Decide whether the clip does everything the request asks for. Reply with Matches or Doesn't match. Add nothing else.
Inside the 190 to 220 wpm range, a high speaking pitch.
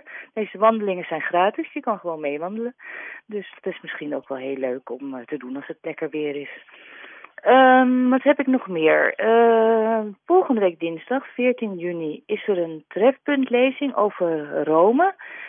Doesn't match